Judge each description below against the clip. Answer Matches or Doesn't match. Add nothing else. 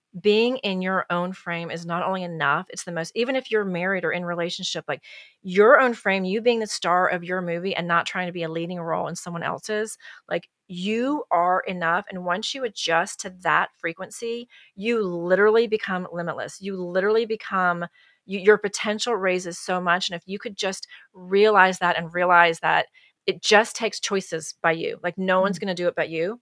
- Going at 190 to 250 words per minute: Matches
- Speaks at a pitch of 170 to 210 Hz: Matches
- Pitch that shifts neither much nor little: Matches